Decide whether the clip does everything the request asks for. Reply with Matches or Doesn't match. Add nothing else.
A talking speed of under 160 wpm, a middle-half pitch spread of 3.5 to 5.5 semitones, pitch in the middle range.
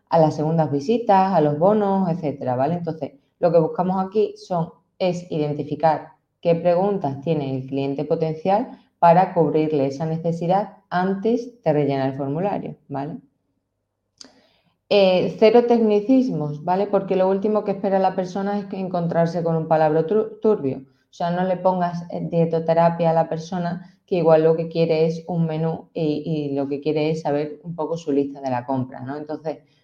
Doesn't match